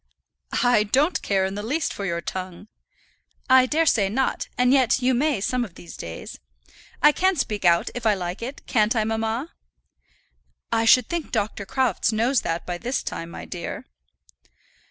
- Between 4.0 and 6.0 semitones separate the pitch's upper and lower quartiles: Yes, average, 5.0 semitones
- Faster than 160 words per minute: Yes, average, 175 wpm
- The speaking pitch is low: No, high, 225 Hz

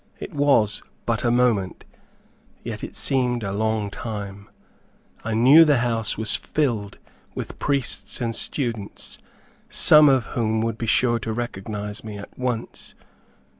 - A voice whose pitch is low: Yes, low, 115 Hz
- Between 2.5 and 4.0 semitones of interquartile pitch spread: Yes, average, 2.8 semitones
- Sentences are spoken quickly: No, average, 140 wpm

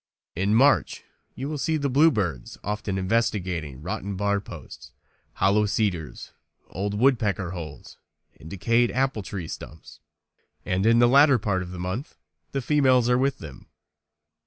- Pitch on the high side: No, low, 105 Hz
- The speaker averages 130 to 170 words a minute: Yes, average, 145 wpm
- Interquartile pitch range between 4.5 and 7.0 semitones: Yes, wide, 5.5 semitones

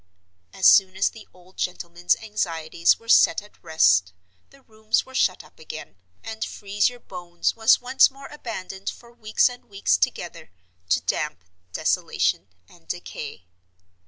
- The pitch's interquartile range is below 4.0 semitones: No, average, 4.9 semitones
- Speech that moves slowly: No, average, 150 wpm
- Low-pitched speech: No, high, 190 Hz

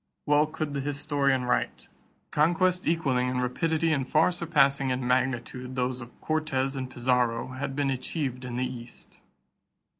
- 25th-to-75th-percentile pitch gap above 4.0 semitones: No, average, 3.1 semitones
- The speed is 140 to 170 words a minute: Yes, average, 150 wpm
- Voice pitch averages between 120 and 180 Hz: Yes, low, 135 Hz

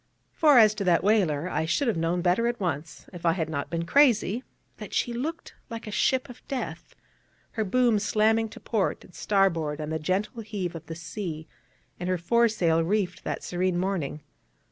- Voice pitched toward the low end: No, medium, 185 Hz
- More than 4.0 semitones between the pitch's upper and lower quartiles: Yes, average, 5.1 semitones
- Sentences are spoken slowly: No, average, 195 wpm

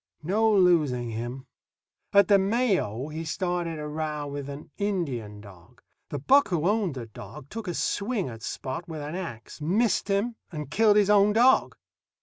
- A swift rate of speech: No, average, 170 wpm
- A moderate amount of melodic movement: No, wide, 7.0 semitones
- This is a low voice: No, medium, 165 Hz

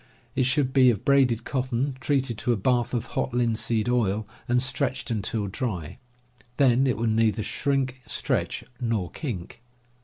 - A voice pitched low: Yes, low, 120 Hz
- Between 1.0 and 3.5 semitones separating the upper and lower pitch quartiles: Yes, average, 2.8 semitones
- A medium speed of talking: Yes, average, 155 wpm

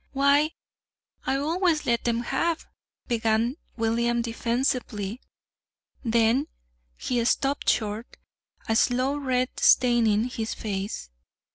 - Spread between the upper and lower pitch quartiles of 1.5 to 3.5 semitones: Yes, average, 3.2 semitones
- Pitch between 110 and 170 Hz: No, high, 240 Hz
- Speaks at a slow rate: Yes, slow, 105 wpm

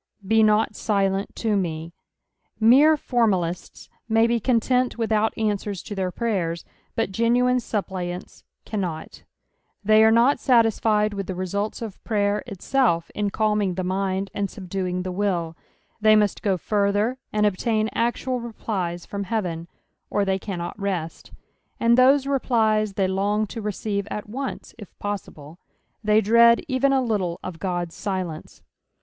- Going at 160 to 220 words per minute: No, average, 150 wpm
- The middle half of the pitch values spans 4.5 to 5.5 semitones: No, average, 3.2 semitones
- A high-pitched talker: Yes, high, 205 Hz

